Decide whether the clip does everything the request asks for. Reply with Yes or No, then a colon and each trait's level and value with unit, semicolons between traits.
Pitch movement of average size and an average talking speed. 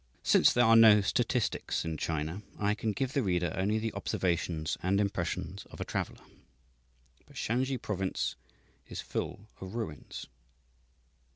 Yes: average, 4.3 semitones; average, 145 wpm